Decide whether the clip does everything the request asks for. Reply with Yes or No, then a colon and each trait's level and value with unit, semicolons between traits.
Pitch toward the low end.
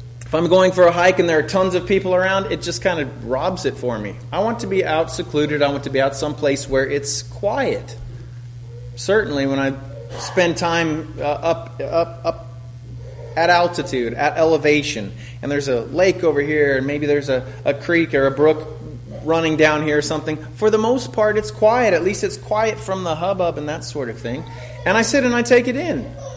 No: medium, 150 Hz